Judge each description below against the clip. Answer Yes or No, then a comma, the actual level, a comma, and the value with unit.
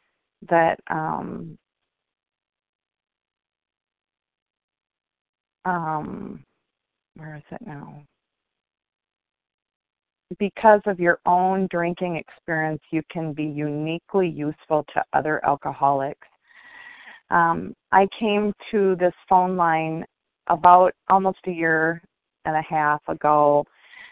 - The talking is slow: Yes, slow, 90 wpm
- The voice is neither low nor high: Yes, medium, 170 Hz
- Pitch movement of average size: Yes, average, 3.5 semitones